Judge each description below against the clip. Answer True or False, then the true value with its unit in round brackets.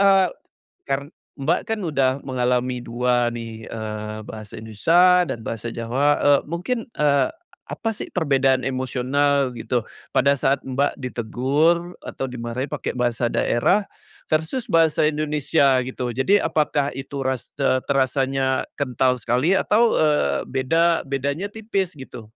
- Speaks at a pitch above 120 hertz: True (135 Hz)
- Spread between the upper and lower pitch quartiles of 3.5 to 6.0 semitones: True (4.1 semitones)